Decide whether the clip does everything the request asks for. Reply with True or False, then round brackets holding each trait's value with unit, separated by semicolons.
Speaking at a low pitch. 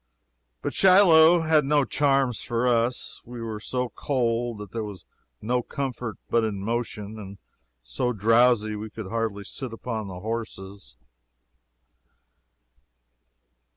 True (115 Hz)